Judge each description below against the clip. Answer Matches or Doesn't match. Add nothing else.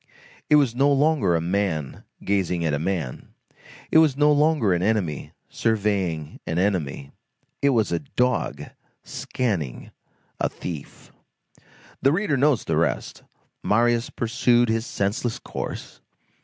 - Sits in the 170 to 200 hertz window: Doesn't match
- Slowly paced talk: Matches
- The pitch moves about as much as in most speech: Doesn't match